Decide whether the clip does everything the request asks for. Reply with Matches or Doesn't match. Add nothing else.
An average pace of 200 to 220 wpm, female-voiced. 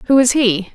Doesn't match